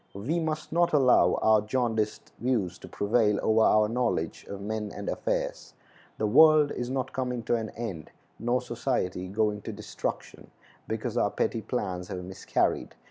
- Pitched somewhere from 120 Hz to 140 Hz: No, low, 110 Hz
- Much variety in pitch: No, average, 3.4 semitones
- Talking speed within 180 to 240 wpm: No, average, 160 wpm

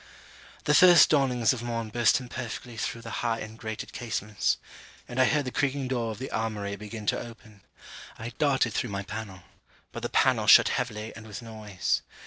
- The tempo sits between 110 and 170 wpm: No, average, 185 wpm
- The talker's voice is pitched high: No, low, 115 Hz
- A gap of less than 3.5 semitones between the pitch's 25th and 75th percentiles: Yes, narrow, 2.6 semitones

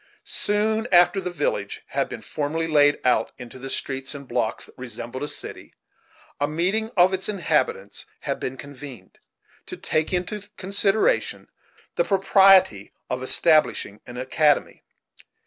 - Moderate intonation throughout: No, wide, 6.7 semitones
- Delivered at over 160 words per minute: No, average, 140 wpm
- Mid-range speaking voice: Yes, medium, 160 Hz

